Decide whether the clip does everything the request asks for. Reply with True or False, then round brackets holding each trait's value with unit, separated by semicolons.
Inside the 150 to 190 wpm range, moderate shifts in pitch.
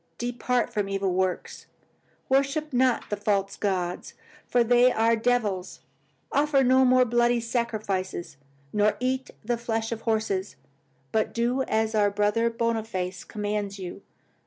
False (135 wpm; 3.3 semitones)